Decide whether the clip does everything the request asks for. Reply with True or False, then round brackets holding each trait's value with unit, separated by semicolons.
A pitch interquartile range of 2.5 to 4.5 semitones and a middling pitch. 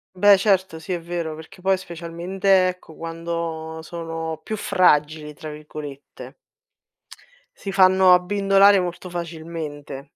True (2.8 semitones; 170 Hz)